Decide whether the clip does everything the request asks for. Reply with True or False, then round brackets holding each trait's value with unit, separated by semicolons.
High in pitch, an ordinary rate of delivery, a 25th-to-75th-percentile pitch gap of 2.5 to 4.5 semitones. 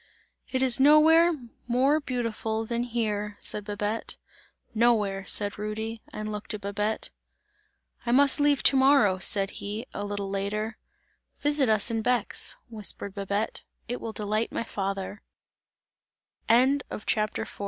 False (220 Hz; 125 wpm; 3.3 semitones)